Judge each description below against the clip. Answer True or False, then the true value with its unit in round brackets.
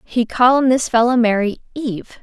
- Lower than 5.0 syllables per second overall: False (5.4 syllables/s)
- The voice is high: True (240 Hz)